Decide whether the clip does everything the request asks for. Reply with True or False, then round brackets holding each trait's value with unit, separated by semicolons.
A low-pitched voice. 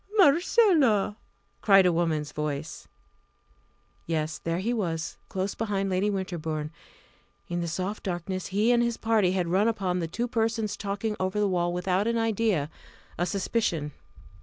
False (190 Hz)